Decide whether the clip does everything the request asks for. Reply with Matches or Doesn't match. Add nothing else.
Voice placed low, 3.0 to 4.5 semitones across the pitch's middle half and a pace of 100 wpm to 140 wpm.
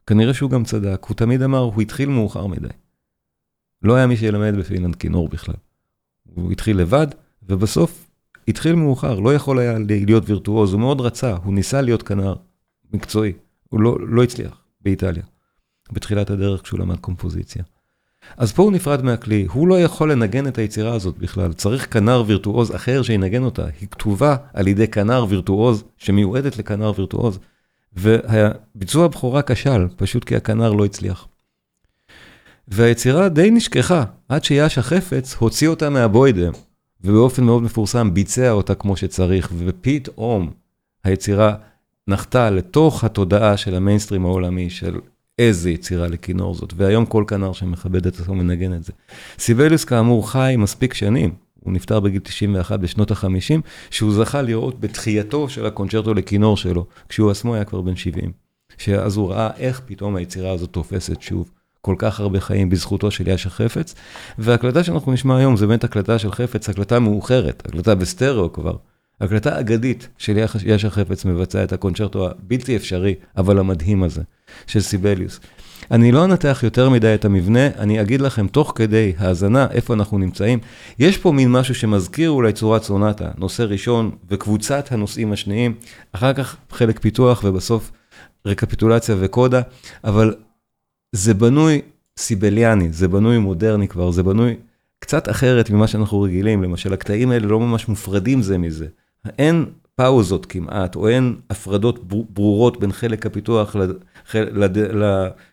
Doesn't match